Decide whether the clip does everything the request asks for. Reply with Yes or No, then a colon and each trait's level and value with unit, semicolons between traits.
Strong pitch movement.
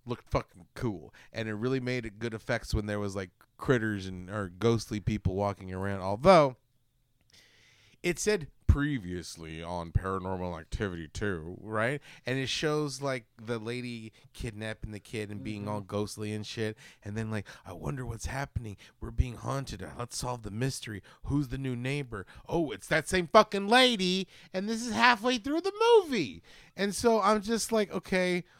Yes: wide, 5.8 semitones